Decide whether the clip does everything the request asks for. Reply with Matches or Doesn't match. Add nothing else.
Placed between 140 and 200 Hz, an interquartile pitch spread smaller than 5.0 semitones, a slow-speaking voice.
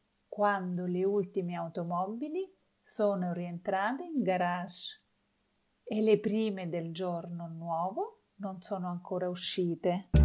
Matches